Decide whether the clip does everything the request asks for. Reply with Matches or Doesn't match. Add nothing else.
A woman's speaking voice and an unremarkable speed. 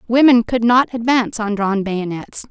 Matches